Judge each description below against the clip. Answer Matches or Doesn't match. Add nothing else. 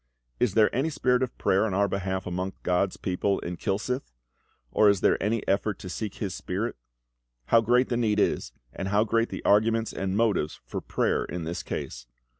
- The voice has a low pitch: Matches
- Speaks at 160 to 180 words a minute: Doesn't match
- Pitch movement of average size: Matches